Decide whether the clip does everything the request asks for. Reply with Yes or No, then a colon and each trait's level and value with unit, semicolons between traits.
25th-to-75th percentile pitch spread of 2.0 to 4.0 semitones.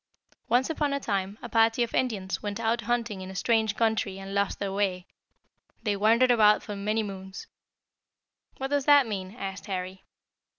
Yes: average, 3.3 semitones